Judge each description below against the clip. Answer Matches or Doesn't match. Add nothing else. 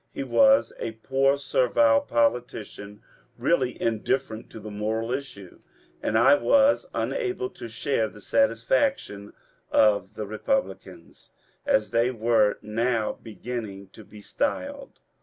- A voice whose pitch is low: Matches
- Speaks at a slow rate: Matches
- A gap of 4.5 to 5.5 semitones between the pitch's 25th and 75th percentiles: Matches